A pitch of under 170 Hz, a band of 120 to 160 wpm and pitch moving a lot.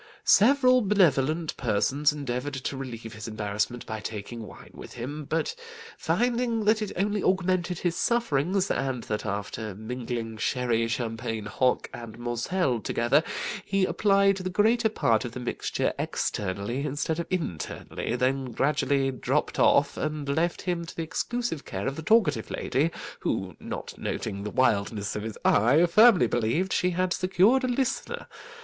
Yes: medium, 140 Hz; average, 155 wpm; wide, 8.2 semitones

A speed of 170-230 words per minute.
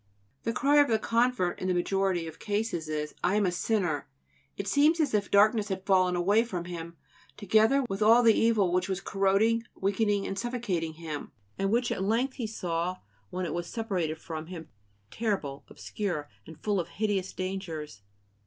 Yes: average, 180 wpm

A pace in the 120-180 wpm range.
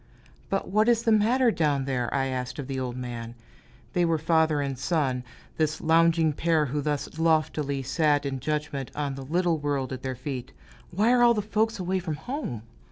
No: average, 195 wpm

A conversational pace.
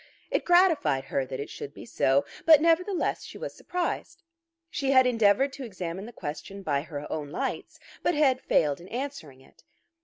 Yes: average, 180 wpm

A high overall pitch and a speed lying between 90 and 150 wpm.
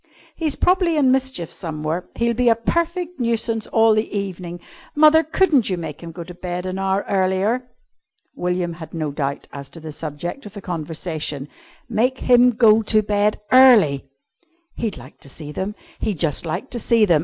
No: high, 200 Hz; average, 180 wpm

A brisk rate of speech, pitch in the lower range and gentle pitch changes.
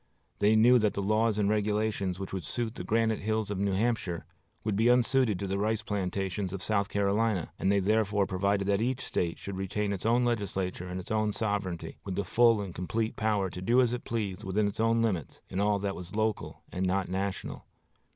Yes: fast, 215 wpm; low, 100 Hz; narrow, 2.3 semitones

